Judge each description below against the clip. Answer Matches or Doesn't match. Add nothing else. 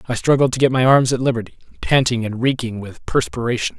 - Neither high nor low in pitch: Doesn't match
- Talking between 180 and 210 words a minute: Matches